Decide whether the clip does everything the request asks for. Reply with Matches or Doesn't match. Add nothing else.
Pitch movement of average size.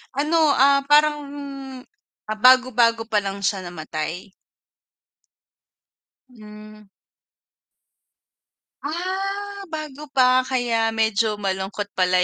Doesn't match